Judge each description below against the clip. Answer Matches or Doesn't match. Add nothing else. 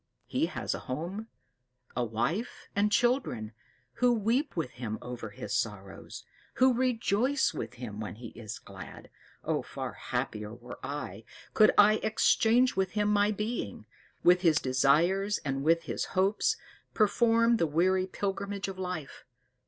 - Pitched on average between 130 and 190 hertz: Matches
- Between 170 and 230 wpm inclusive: Doesn't match